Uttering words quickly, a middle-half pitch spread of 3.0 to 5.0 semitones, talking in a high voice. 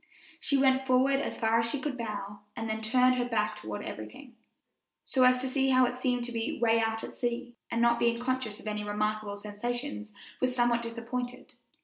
No: fast, 215 wpm; narrow, 2.6 semitones; high, 235 Hz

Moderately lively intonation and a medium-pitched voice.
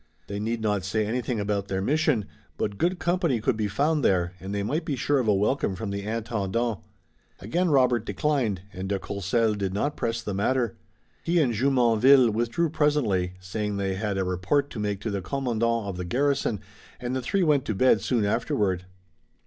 No: average, 4.8 semitones; low, 110 Hz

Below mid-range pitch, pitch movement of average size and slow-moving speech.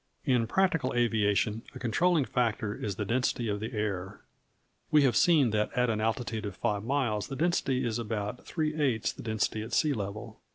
No: low, 115 Hz; average, 3.7 semitones; average, 190 wpm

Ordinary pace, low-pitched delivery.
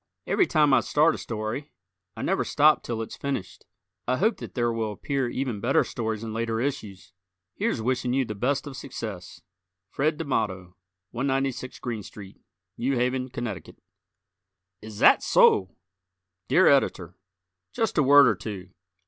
Yes: average, 155 wpm; low, 120 Hz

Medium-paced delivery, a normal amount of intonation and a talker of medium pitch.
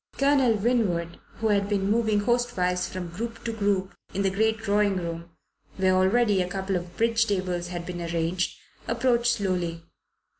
No: average, 160 wpm; average, 3.8 semitones; high, 195 Hz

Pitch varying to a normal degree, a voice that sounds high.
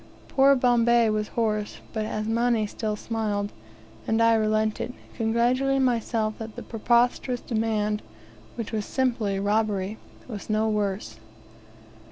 No: narrow, 1.9 semitones; high, 220 Hz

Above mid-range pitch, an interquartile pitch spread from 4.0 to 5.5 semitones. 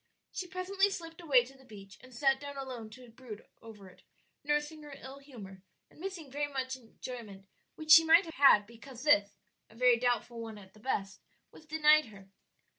Yes: very high, 260 Hz; average, 5.1 semitones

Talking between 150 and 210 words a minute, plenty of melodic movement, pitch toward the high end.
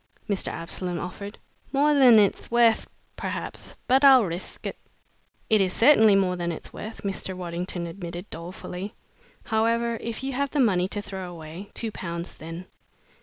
No: average, 160 wpm; average, 4.6 semitones; high, 195 Hz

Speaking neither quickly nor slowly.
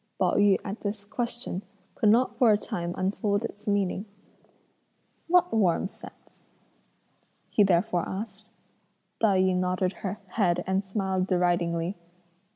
No: slow, 130 wpm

